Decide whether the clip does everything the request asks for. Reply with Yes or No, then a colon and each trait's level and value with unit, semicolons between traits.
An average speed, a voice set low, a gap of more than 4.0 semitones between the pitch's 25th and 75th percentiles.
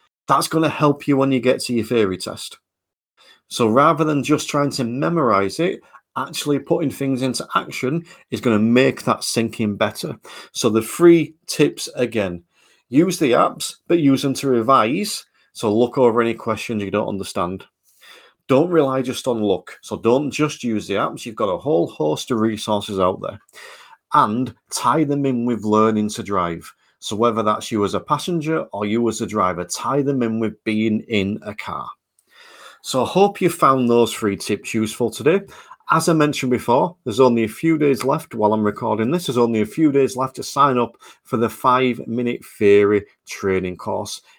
Yes: average, 190 wpm; low, 120 Hz; average, 4.7 semitones